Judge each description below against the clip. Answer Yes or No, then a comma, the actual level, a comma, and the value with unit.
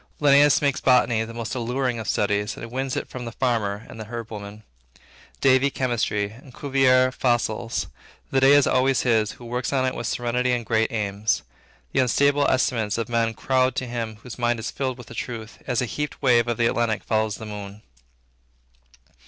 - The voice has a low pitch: Yes, low, 120 Hz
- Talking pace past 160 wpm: Yes, average, 195 wpm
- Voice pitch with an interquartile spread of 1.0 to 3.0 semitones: Yes, average, 2.7 semitones